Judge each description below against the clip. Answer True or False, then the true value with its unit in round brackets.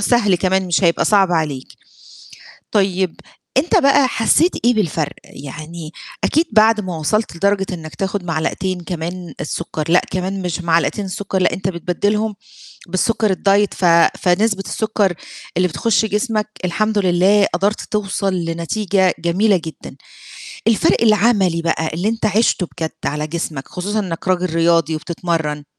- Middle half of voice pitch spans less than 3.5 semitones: False (3.8 semitones)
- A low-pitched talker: False (185 Hz)